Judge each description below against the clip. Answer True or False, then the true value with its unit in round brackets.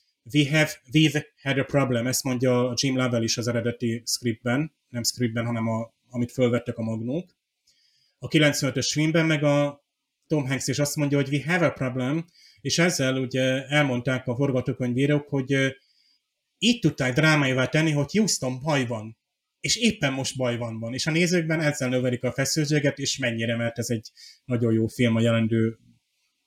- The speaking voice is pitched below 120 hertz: False (130 Hz)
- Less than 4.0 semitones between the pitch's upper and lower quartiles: True (3.4 semitones)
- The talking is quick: True (170 wpm)